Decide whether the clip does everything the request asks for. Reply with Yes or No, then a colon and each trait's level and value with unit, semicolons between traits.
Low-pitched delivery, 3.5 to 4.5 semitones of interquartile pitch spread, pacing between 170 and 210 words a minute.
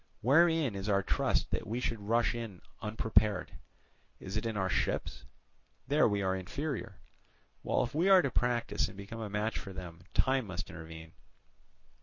Yes: low, 110 Hz; average, 4.1 semitones; average, 175 wpm